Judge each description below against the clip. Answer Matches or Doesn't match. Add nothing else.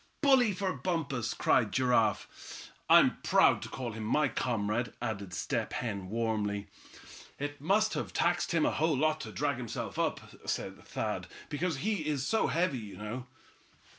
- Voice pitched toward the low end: Matches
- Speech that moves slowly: Doesn't match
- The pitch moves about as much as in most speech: Doesn't match